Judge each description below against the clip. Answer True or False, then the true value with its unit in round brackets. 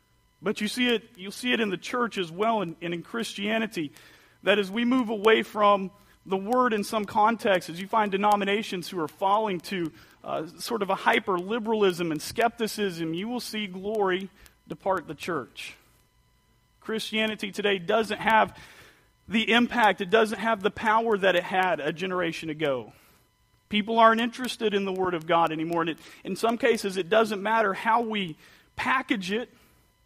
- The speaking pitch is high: True (205 Hz)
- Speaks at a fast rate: False (175 wpm)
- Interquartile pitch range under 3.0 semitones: False (3.4 semitones)